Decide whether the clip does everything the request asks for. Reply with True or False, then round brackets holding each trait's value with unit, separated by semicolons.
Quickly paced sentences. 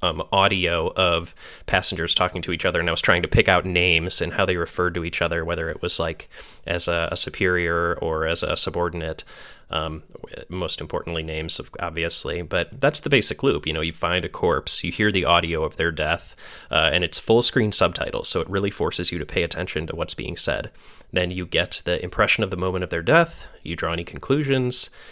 True (220 wpm)